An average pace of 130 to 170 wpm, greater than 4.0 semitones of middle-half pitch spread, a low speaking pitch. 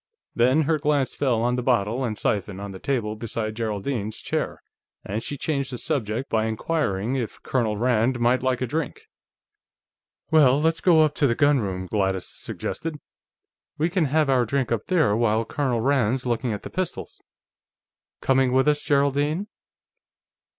Yes: average, 165 wpm; average, 4.6 semitones; low, 125 Hz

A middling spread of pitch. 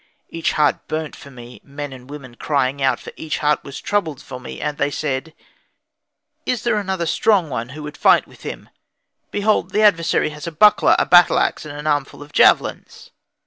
Yes: average, 3.3 semitones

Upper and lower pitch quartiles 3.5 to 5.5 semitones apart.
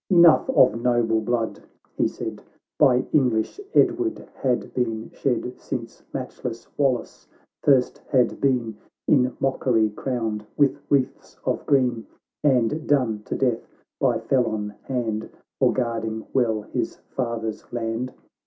No: average, 2.9 semitones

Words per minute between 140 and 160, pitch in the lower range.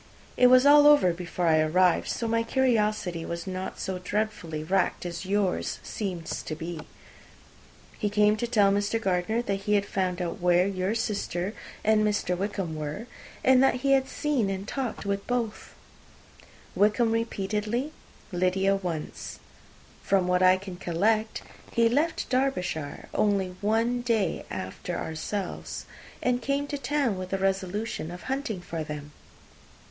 No: average, 155 wpm; high, 200 Hz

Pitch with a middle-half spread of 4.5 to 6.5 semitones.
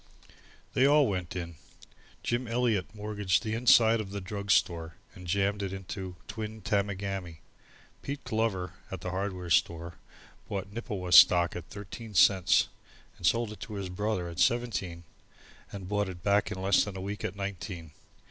No: average, 2.9 semitones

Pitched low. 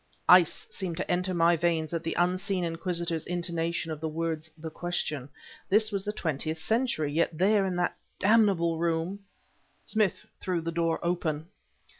No: medium, 170 Hz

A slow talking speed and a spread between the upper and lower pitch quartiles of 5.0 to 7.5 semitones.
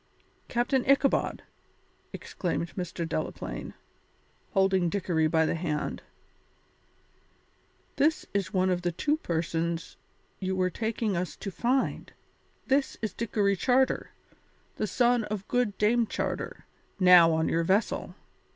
Yes: slow, 120 wpm; wide, 5.4 semitones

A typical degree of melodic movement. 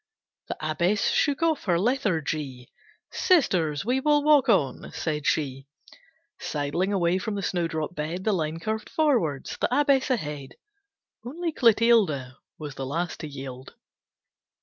No: wide, 8.2 semitones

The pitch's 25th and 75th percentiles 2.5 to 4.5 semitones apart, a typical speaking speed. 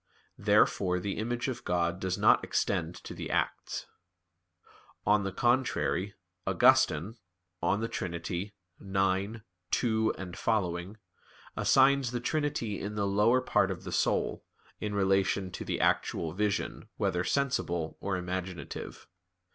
No: average, 3.8 semitones; slow, 125 wpm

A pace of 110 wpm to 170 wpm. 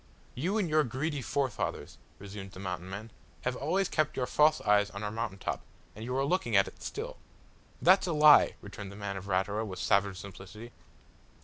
No: average, 195 wpm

